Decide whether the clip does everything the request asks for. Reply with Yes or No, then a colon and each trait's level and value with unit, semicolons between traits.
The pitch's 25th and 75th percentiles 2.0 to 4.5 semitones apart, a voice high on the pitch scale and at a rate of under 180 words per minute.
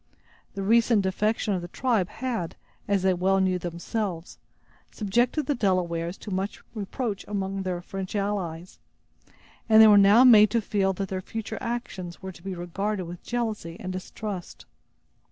Yes: average, 2.9 semitones; high, 195 Hz; average, 160 wpm